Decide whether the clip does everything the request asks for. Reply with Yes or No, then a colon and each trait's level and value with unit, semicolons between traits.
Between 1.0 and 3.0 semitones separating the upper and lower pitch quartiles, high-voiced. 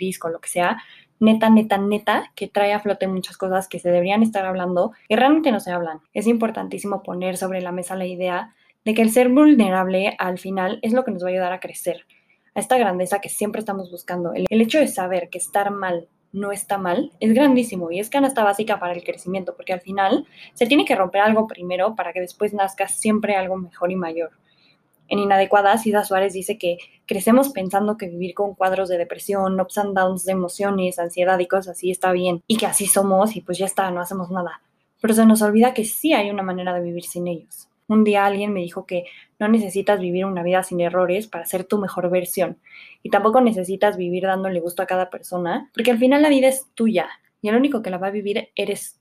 Yes: average, 2.7 semitones; high, 195 Hz